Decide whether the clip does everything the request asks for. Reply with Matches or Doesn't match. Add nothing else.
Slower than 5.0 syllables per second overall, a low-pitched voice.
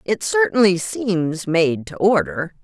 Doesn't match